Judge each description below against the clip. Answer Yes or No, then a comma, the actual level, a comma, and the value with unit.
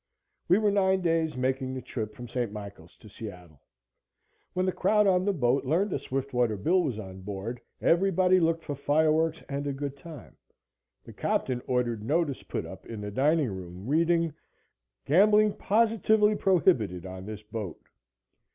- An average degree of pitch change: No, wide, 8.4 semitones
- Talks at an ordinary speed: Yes, average, 160 wpm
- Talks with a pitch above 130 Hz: Yes, medium, 140 Hz